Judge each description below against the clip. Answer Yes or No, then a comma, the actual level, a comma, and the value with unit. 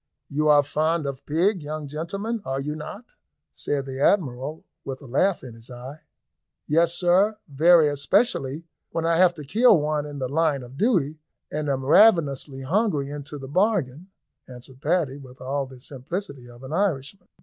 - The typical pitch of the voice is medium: Yes, medium, 150 Hz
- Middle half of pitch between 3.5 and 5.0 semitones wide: Yes, average, 4.4 semitones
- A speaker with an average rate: Yes, average, 170 wpm